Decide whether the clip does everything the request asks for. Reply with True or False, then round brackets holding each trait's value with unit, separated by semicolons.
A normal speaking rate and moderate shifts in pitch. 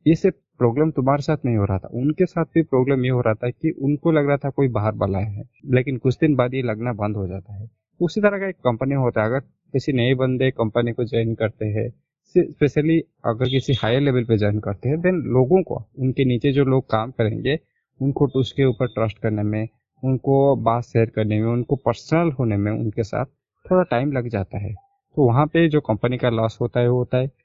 False (225 wpm; 4.0 semitones)